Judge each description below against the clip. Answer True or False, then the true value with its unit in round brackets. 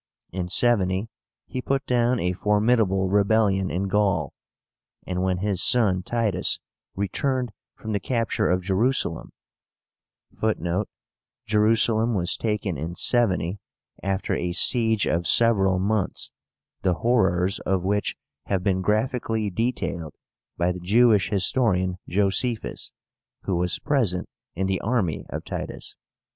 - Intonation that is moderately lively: True (3.6 semitones)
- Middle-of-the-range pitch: False (100 Hz)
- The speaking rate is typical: False (125 wpm)